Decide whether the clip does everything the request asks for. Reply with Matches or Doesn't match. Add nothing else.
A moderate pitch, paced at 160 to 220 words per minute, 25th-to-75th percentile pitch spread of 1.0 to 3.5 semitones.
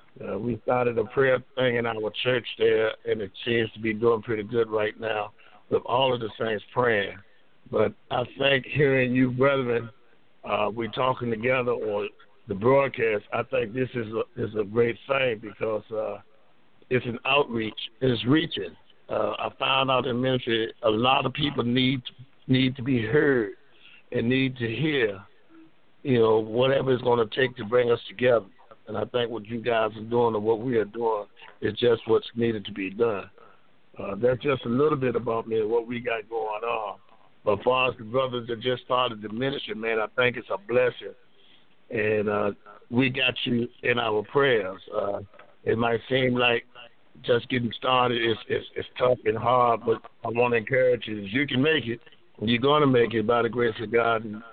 Doesn't match